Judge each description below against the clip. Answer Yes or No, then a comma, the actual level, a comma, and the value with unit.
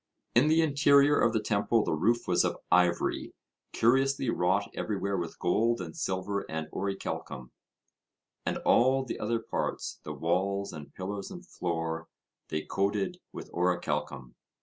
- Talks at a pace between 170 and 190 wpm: No, average, 145 wpm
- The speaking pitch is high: No, low, 100 Hz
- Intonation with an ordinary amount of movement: No, wide, 5.8 semitones